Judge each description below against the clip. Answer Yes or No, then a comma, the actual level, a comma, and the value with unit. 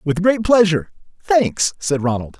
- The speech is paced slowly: Yes, slow, 125 wpm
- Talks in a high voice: No, medium, 170 Hz